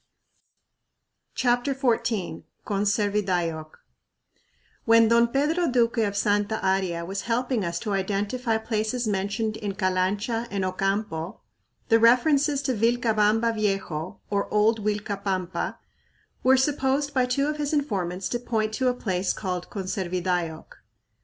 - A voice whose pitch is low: No, high, 215 Hz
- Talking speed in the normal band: No, slow, 120 wpm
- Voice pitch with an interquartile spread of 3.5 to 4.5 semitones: Yes, average, 4.0 semitones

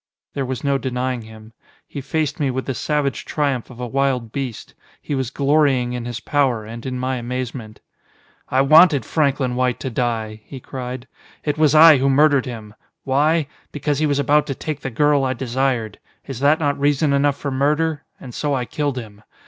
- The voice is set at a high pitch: No, low, 135 Hz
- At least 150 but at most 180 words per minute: No, average, 195 wpm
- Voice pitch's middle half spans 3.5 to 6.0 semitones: No, average, 2.7 semitones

